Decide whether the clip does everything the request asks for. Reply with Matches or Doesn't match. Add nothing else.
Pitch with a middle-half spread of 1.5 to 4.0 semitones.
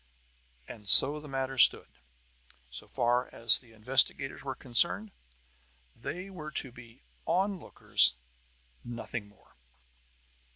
Doesn't match